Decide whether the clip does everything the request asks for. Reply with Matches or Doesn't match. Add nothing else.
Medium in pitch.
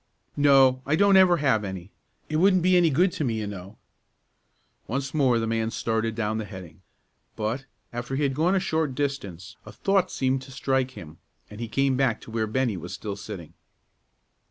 Doesn't match